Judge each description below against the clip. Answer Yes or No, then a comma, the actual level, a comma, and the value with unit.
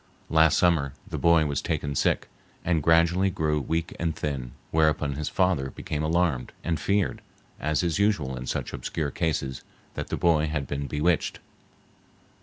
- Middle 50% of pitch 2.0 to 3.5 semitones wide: Yes, average, 2.8 semitones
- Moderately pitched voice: No, very low, 80 Hz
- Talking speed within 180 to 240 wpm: No, average, 160 wpm